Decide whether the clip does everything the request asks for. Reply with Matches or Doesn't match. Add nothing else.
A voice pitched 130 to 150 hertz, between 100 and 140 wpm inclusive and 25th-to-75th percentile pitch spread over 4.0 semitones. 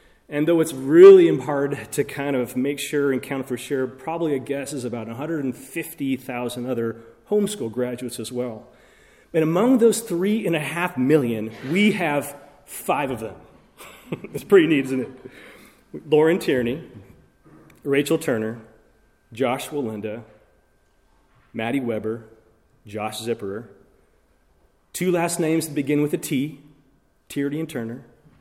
Matches